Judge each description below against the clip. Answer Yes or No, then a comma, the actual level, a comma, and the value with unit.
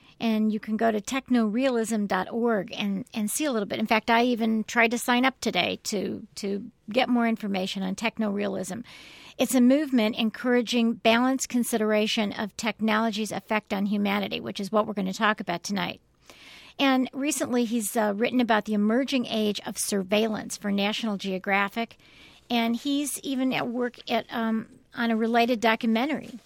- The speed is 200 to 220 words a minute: No, average, 165 wpm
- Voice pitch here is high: Yes, high, 225 Hz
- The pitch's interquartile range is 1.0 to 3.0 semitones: Yes, narrow, 2.5 semitones